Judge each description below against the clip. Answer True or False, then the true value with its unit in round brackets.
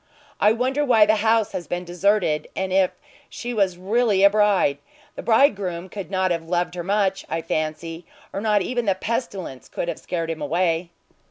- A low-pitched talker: False (190 Hz)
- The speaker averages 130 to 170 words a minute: False (185 wpm)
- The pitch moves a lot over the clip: False (3.7 semitones)